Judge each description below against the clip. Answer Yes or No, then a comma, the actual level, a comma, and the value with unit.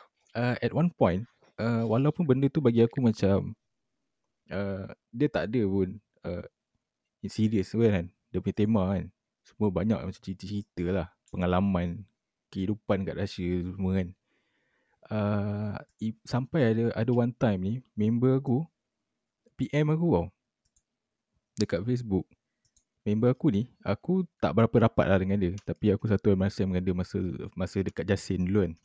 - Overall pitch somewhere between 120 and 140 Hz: No, low, 105 Hz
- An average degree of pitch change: Yes, average, 3.9 semitones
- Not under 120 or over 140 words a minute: No, fast, 155 wpm